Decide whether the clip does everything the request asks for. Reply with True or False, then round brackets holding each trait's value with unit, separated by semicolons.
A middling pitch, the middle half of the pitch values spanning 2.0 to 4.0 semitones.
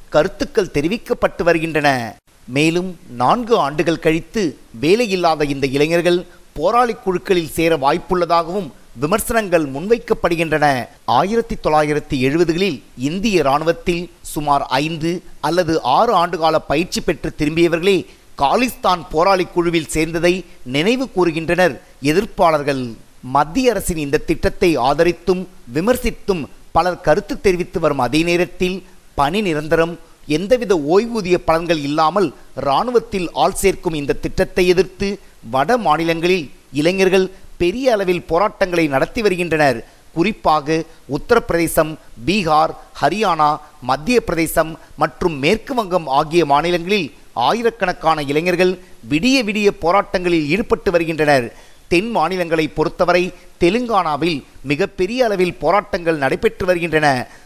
True (175 Hz; 3.7 semitones)